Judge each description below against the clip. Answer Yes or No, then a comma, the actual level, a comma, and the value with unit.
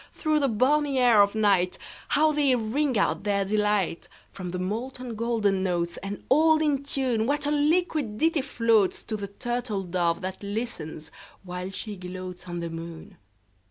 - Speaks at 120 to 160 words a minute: Yes, average, 140 wpm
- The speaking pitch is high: Yes, high, 215 Hz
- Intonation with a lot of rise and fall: Yes, wide, 6.3 semitones